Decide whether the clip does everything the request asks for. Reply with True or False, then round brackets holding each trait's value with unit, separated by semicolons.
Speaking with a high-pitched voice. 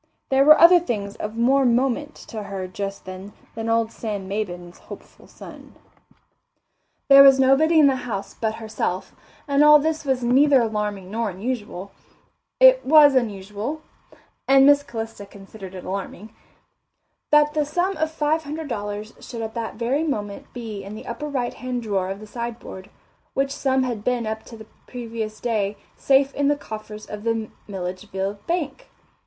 True (230 Hz)